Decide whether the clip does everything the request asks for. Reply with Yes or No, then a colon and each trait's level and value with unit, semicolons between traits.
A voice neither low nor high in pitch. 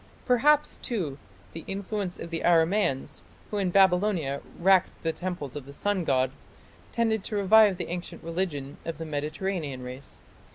Yes: medium, 175 Hz